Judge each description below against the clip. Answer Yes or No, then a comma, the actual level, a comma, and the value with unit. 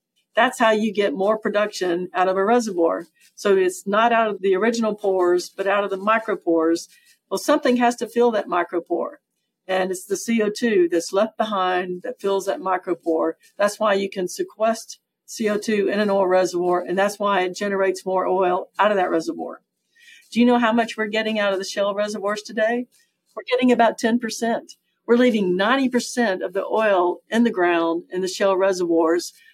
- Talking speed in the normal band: Yes, average, 185 wpm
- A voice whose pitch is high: Yes, high, 205 Hz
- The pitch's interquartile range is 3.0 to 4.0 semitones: Yes, average, 3.6 semitones